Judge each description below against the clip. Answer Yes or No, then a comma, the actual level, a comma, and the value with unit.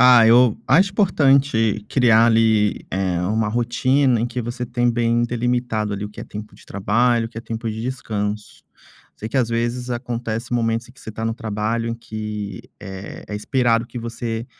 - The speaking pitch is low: Yes, low, 115 Hz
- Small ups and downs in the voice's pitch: Yes, narrow, 2.0 semitones